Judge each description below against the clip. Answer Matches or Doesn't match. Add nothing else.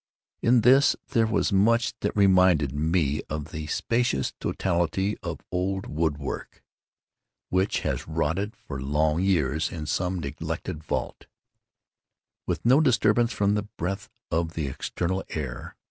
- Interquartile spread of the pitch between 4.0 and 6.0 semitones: Matches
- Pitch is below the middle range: Matches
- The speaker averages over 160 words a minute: Doesn't match